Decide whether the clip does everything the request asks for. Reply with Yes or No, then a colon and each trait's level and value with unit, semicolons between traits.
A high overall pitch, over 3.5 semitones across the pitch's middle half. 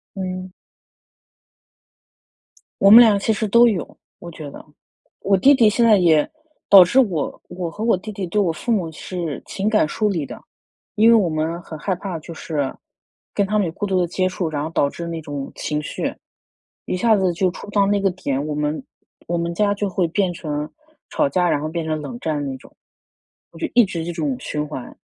No: medium, 180 Hz; average, 4.5 semitones